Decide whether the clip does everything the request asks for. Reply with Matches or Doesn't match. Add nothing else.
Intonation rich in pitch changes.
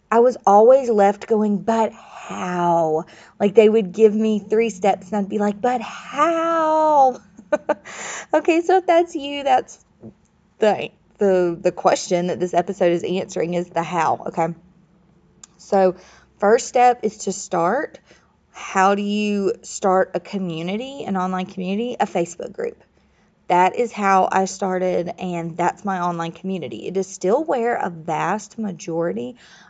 Doesn't match